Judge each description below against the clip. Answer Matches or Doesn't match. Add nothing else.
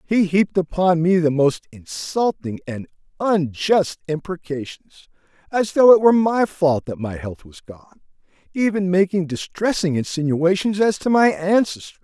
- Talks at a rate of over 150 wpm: Doesn't match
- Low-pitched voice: Doesn't match